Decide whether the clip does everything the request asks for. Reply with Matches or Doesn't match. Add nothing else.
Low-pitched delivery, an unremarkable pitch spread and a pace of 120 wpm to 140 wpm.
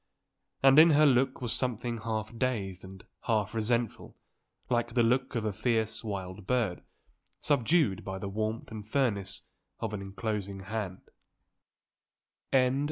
Matches